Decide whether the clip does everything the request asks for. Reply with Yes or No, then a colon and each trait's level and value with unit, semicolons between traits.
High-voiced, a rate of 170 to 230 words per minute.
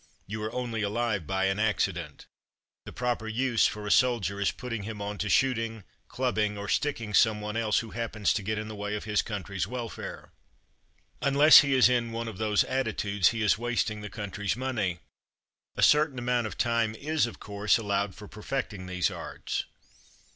No: low, 110 Hz; average, 185 wpm